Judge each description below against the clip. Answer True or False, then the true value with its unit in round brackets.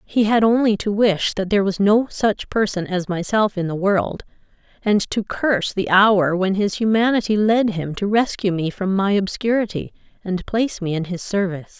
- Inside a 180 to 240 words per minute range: True (195 wpm)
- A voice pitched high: True (200 Hz)